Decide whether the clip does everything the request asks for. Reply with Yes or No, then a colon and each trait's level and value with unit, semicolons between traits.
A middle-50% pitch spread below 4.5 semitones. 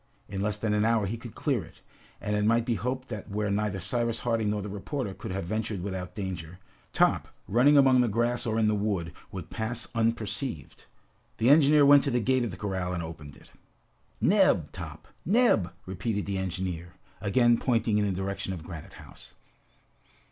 Yes: average, 3.8 semitones